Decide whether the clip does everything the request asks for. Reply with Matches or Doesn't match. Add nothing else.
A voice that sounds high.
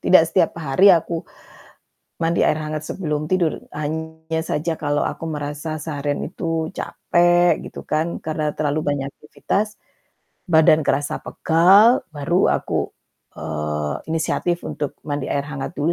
Doesn't match